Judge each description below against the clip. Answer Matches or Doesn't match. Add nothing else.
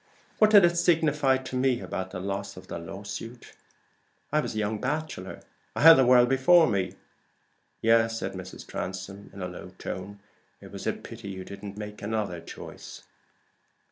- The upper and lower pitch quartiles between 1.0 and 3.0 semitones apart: Doesn't match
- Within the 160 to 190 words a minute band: Matches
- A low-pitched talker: Matches